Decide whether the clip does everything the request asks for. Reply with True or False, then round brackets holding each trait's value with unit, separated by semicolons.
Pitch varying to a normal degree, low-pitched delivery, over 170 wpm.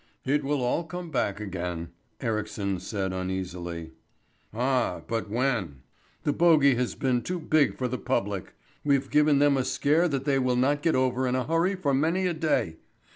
False (6.0 semitones; 130 Hz; 180 wpm)